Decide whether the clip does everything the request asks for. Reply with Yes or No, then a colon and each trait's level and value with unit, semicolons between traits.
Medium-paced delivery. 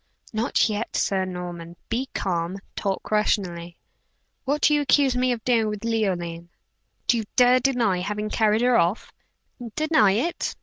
Yes: average, 150 wpm